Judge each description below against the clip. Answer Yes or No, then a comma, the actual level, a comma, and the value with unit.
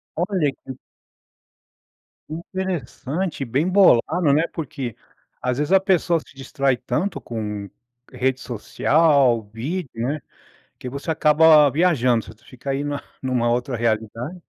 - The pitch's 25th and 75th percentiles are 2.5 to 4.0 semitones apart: No, average, 4.9 semitones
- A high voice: No, medium, 140 Hz